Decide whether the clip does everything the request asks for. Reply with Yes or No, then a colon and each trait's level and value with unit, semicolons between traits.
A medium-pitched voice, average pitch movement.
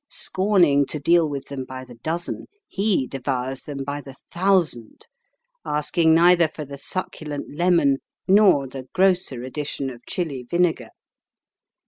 Yes: medium, 150 Hz; average, 4.4 semitones